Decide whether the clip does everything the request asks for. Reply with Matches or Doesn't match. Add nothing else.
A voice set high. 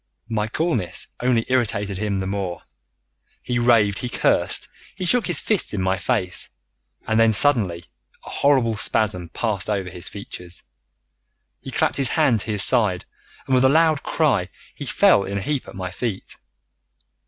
Doesn't match